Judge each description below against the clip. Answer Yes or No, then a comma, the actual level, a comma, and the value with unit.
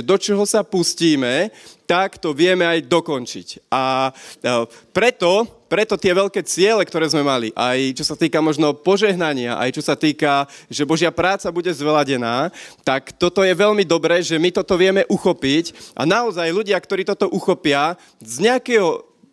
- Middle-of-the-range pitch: Yes, medium, 170 Hz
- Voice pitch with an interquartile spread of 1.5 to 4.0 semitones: No, average, 4.8 semitones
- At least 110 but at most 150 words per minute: No, fast, 165 wpm